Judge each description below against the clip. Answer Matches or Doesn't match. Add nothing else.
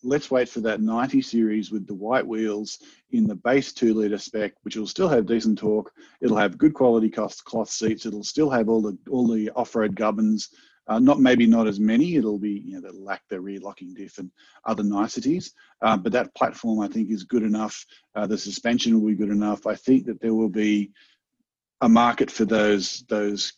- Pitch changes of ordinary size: Doesn't match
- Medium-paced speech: Doesn't match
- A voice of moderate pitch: Doesn't match